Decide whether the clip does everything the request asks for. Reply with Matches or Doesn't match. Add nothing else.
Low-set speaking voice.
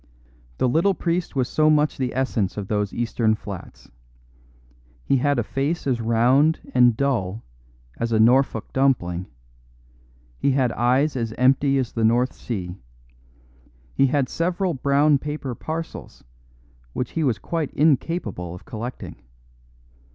Matches